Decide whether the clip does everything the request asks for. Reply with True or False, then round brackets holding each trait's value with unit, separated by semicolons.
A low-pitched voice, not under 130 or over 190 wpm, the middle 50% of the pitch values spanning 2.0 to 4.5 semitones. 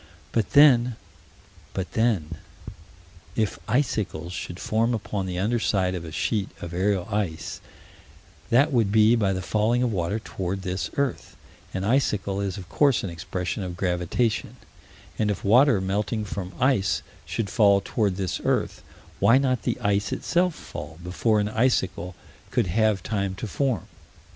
True (100 Hz; 155 wpm; 3.8 semitones)